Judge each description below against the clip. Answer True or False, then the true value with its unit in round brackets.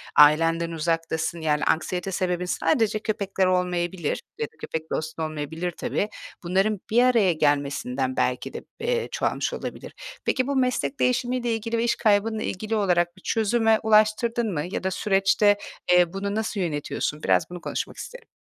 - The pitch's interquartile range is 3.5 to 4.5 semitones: False (5.0 semitones)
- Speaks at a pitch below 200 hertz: True (190 Hz)